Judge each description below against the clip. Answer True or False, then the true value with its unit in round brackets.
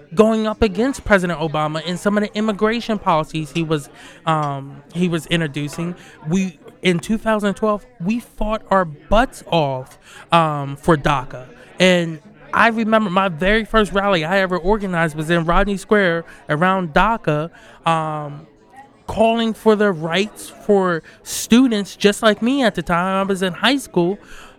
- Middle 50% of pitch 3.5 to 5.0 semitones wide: True (4.7 semitones)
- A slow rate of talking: False (150 wpm)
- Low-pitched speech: False (185 Hz)